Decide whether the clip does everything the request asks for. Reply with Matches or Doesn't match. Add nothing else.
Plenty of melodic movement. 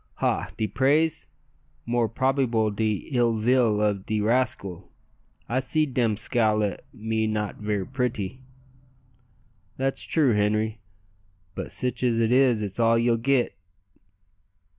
Doesn't match